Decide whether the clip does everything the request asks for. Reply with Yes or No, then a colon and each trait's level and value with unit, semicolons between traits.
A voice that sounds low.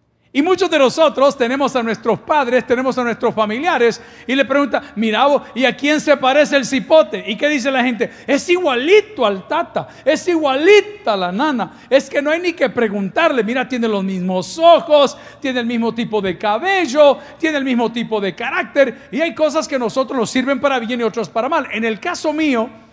No: very high, 265 Hz